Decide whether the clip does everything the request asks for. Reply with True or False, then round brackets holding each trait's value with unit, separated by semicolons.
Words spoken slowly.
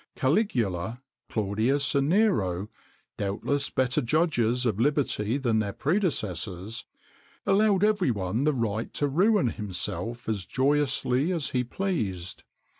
True (125 wpm)